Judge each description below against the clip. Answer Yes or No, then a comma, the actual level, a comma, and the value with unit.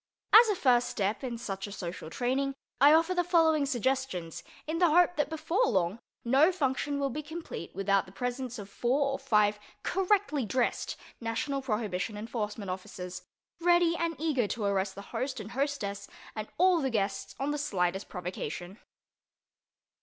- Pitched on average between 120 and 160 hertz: No, very high, 255 Hz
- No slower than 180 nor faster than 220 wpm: No, average, 165 wpm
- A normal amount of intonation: No, wide, 7.1 semitones